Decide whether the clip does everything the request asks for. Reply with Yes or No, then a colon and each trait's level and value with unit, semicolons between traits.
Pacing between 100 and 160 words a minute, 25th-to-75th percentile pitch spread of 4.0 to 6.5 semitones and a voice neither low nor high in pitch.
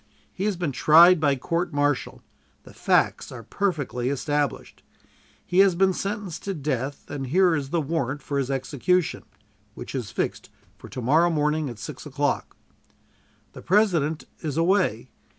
Yes: average, 155 wpm; average, 4.6 semitones; medium, 155 Hz